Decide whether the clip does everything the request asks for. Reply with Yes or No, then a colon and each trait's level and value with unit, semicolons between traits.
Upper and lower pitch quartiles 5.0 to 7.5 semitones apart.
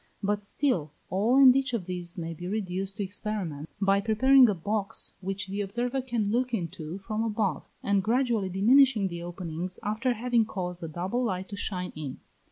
No: average, 4.2 semitones